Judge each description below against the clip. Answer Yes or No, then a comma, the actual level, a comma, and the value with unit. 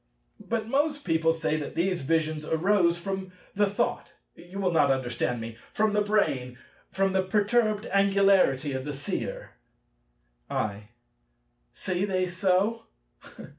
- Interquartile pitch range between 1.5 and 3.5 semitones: No, average, 4.6 semitones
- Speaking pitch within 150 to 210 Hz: Yes, medium, 185 Hz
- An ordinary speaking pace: No, slow, 125 wpm